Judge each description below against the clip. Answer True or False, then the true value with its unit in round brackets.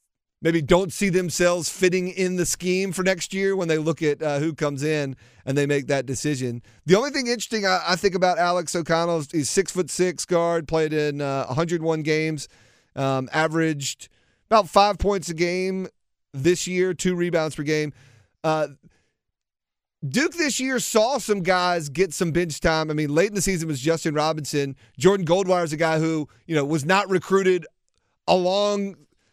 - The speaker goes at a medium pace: True (180 wpm)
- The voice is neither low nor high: True (165 Hz)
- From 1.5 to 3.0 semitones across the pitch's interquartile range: False (3.6 semitones)